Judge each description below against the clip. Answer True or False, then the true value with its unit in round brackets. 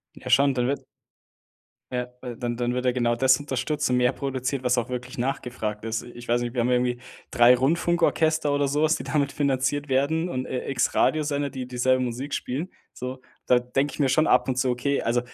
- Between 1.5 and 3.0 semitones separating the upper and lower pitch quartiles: True (2.5 semitones)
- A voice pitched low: True (130 Hz)